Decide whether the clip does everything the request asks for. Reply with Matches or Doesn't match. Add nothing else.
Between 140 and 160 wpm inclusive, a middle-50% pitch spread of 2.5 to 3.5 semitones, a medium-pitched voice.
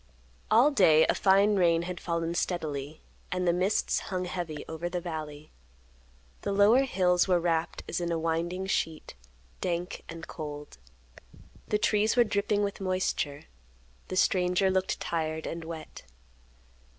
Matches